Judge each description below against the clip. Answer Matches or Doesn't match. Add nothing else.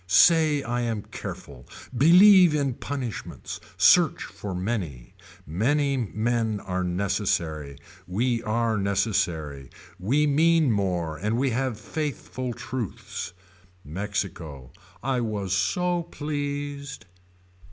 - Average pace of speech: Doesn't match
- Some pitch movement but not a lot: Doesn't match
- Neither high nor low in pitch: Doesn't match